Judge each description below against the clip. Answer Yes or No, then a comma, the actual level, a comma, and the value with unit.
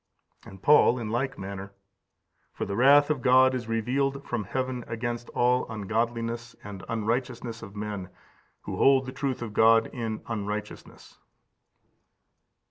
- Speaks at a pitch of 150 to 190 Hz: No, low, 115 Hz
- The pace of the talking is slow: No, average, 145 wpm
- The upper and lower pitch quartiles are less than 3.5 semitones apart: Yes, average, 3.1 semitones